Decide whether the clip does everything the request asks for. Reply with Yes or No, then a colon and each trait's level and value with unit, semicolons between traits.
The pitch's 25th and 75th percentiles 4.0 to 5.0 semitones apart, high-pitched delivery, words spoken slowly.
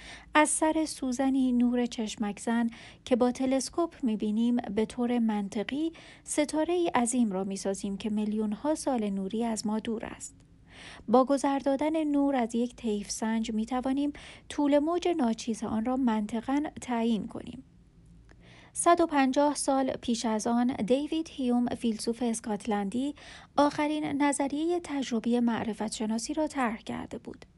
No: average, 4.3 semitones; high, 245 Hz; average, 140 wpm